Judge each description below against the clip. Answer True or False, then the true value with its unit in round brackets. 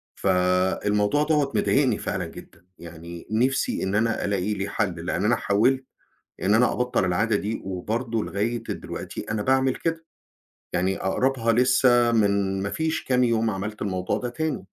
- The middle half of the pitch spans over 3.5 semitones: True (4.5 semitones)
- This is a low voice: True (110 Hz)